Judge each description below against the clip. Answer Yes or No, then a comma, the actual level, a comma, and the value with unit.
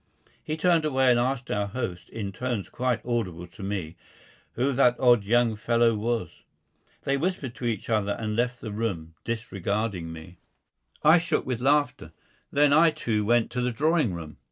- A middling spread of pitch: Yes, average, 4.1 semitones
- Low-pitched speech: Yes, low, 115 Hz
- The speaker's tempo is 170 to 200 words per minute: Yes, average, 175 wpm